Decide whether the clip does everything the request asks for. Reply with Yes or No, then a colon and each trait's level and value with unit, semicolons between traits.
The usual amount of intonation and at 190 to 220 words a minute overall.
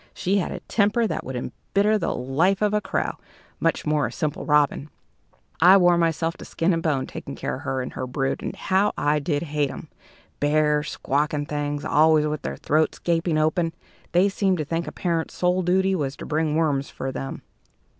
Yes: average, 3.4 semitones; average, 200 wpm